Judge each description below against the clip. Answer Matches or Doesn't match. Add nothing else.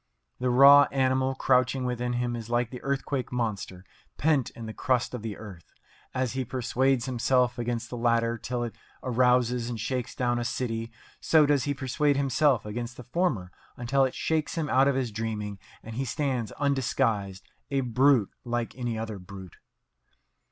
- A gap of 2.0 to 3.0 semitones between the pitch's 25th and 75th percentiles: Matches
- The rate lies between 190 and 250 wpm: Doesn't match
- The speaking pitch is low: Matches